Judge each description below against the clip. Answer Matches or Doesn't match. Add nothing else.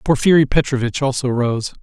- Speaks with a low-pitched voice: Matches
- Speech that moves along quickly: Doesn't match